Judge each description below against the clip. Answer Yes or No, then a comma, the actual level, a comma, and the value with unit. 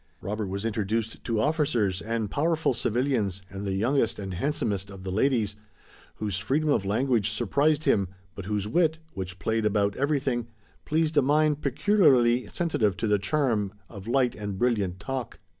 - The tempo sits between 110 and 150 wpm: No, average, 160 wpm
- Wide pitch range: Yes, wide, 5.7 semitones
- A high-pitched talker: No, low, 115 Hz